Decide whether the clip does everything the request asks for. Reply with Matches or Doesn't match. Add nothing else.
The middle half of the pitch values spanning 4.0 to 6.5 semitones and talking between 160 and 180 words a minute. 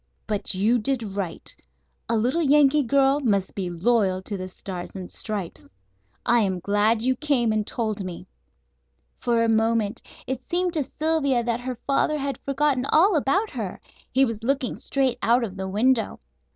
Matches